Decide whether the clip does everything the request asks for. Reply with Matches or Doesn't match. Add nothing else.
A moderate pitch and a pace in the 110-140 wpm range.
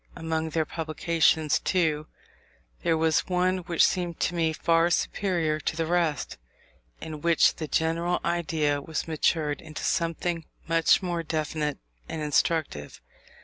Matches